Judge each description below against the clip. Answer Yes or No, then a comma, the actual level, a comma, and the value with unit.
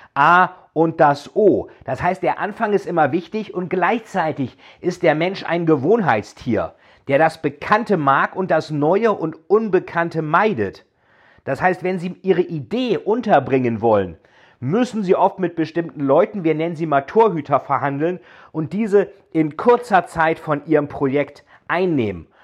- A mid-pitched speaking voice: Yes, medium, 165 Hz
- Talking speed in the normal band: Yes, average, 150 wpm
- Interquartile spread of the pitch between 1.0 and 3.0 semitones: No, average, 4.2 semitones